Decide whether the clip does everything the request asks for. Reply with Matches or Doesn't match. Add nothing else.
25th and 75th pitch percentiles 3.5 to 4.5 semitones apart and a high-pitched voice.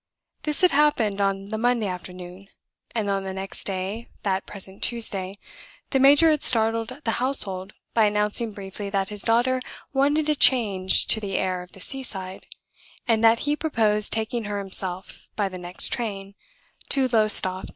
Matches